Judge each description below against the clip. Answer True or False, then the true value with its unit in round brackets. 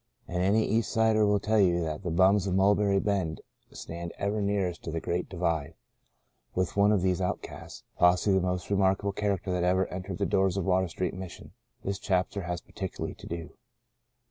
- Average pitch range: False (2.2 semitones)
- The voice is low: True (95 Hz)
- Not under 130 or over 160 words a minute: False (200 wpm)